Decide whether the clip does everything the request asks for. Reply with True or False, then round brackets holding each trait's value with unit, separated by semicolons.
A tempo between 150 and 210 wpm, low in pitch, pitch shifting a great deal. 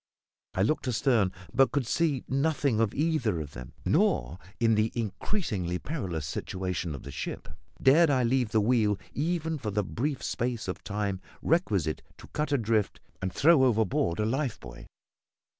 True (160 wpm; 115 Hz; 6.7 semitones)